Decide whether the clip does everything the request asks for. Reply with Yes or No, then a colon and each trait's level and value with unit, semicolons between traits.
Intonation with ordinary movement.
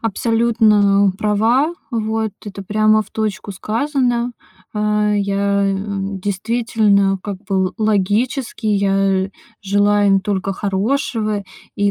No: narrow, 2.0 semitones